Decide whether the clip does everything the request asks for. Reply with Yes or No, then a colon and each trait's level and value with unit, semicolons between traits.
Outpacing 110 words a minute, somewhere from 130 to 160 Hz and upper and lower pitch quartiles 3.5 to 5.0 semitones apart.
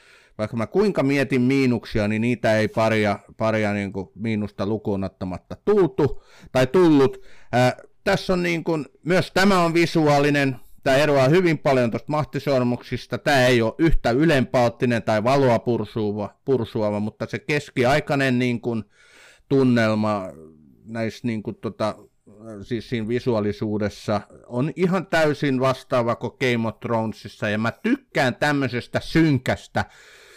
No: average, 130 wpm; low, 120 Hz; average, 4.2 semitones